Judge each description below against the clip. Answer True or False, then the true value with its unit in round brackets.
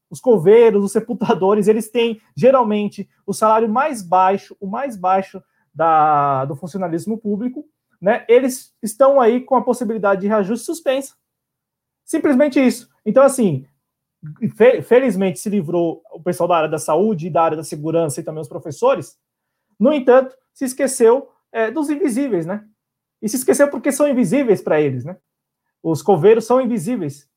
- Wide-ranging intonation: True (6.1 semitones)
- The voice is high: True (215 Hz)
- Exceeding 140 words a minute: True (155 wpm)